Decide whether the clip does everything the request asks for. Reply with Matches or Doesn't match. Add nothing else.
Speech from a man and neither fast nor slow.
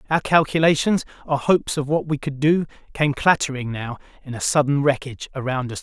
Matches